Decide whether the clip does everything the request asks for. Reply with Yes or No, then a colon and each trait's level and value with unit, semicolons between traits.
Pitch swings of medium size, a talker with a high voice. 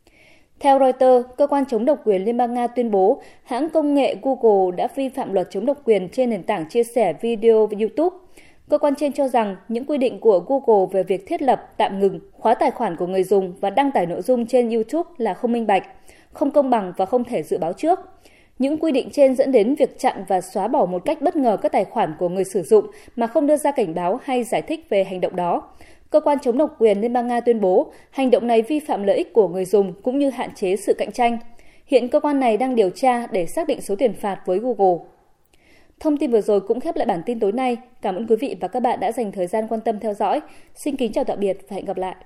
No: wide, 6.0 semitones; high, 240 Hz